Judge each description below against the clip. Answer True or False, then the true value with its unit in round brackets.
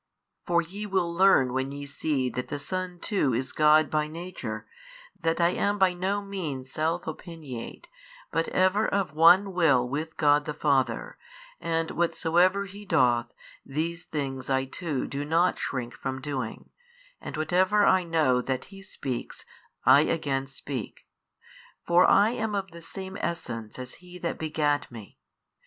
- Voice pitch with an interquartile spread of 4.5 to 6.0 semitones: True (5.1 semitones)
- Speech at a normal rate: True (155 wpm)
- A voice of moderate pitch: True (160 Hz)